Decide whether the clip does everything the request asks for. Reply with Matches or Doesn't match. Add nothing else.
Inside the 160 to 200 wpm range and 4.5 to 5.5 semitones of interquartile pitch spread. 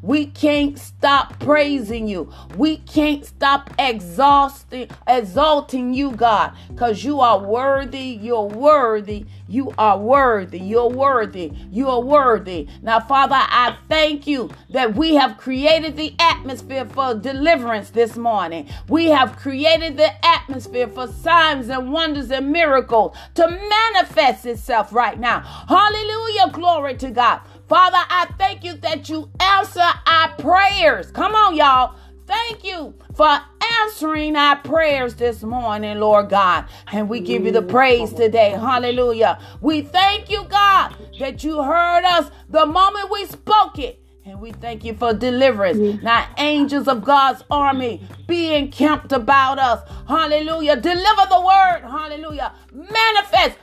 Doesn't match